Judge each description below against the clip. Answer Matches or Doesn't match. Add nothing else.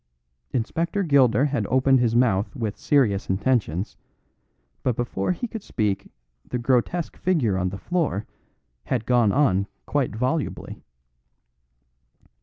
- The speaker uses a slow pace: Matches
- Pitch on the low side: Matches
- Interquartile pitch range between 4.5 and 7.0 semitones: Matches